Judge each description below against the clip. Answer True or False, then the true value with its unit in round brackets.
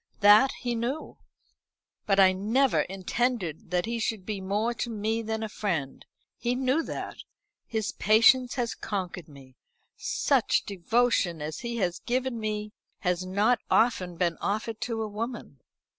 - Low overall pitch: False (215 Hz)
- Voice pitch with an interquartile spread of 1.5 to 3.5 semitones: False (4.1 semitones)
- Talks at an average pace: True (150 wpm)